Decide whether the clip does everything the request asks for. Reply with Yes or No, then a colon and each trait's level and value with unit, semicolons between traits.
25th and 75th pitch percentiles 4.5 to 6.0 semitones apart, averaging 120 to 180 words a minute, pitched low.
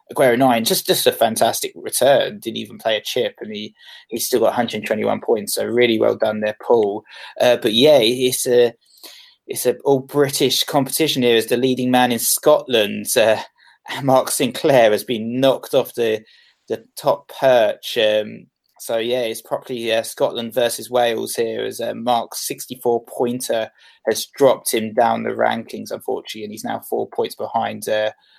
No: average, 3.5 semitones; average, 175 wpm; low, 120 Hz